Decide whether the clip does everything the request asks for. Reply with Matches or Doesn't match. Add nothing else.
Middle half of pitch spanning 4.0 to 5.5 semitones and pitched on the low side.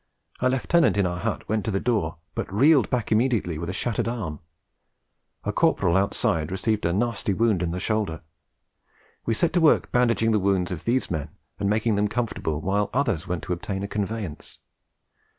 Matches